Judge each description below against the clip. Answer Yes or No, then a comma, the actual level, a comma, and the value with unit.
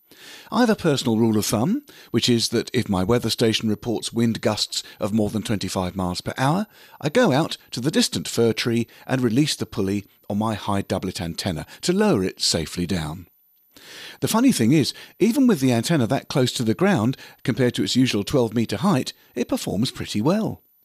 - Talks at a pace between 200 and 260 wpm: Yes, fast, 205 wpm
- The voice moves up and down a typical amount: Yes, average, 4.1 semitones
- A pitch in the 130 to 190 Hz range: No, low, 115 Hz